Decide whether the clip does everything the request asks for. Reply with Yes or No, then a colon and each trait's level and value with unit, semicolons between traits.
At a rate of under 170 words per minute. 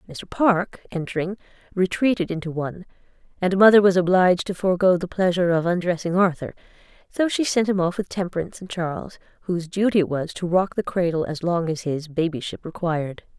No: average, 180 wpm